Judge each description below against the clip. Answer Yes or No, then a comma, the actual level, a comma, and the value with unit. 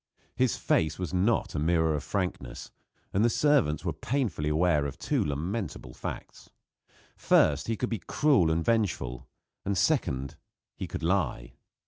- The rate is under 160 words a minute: Yes, average, 150 wpm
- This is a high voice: No, very low, 85 Hz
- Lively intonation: Yes, wide, 6.4 semitones